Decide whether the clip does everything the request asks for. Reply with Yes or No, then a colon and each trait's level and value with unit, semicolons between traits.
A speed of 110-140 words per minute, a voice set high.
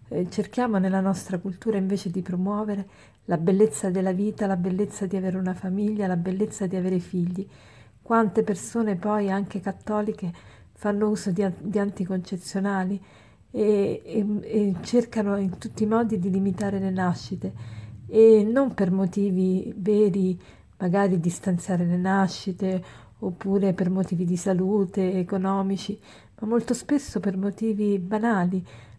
Yes: average, 135 wpm; high, 195 Hz